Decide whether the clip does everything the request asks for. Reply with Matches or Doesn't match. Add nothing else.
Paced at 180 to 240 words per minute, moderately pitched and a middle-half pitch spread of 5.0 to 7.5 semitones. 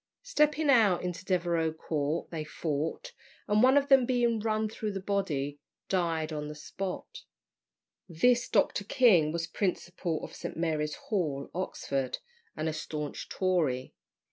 Doesn't match